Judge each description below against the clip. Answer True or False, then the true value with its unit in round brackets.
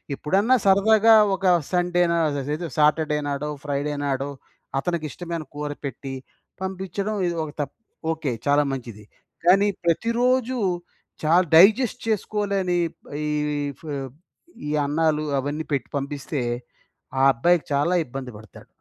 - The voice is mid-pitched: True (160 Hz)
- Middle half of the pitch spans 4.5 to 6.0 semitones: True (5.2 semitones)